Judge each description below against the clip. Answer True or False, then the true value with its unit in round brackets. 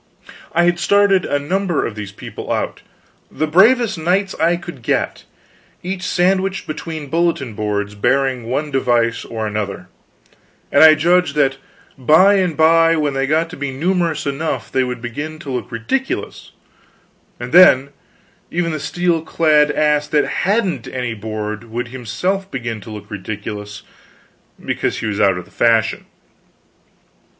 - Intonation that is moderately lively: False (6.8 semitones)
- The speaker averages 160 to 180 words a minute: False (150 wpm)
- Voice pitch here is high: False (145 Hz)